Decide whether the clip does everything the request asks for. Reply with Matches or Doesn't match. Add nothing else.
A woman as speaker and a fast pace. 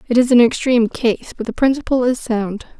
Matches